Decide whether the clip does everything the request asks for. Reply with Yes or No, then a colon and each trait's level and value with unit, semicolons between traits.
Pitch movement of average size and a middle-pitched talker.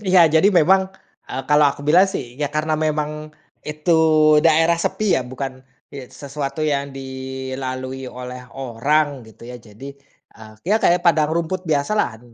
Yes: average, 3.3 semitones; medium, 145 Hz